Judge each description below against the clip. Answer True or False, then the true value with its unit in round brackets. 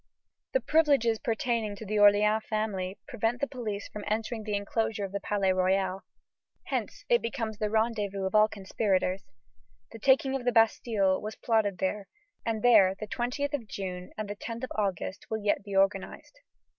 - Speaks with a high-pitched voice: True (215 Hz)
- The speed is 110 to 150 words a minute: False (175 wpm)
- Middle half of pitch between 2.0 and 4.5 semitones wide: True (2.6 semitones)